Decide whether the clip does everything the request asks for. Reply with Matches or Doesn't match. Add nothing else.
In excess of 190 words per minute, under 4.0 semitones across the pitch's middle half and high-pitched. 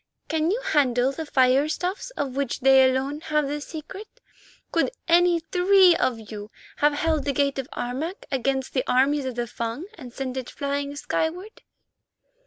Doesn't match